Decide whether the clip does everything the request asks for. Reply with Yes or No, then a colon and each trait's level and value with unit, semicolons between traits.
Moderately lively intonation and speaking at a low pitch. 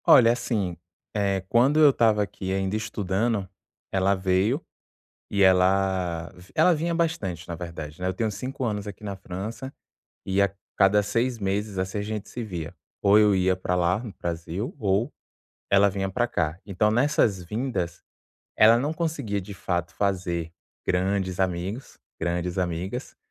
Yes: average, 3.4 semitones; low, 100 Hz